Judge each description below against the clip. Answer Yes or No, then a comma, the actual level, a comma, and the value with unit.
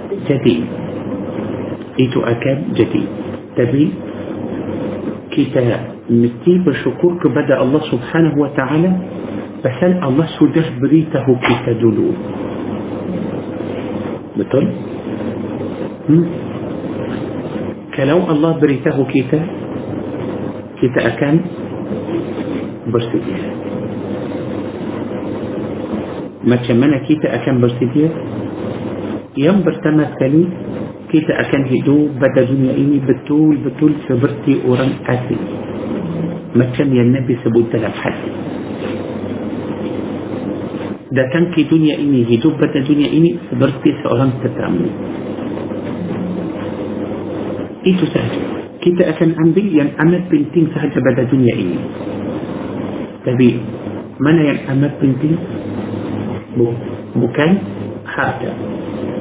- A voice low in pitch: No, medium, 145 Hz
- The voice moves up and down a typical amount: Yes, average, 4.2 semitones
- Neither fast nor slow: No, slow, 80 wpm